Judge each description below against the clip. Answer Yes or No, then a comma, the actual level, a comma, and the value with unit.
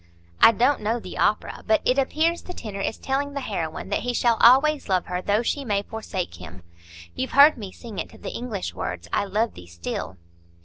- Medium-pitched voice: No, high, 220 Hz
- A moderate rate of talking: No, fast, 215 wpm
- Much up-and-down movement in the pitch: Yes, wide, 5.7 semitones